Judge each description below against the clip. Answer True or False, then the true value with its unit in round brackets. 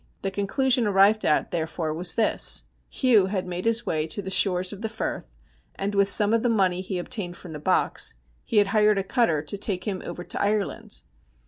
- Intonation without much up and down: False (3.1 semitones)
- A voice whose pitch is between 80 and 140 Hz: False (195 Hz)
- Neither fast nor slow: False (215 wpm)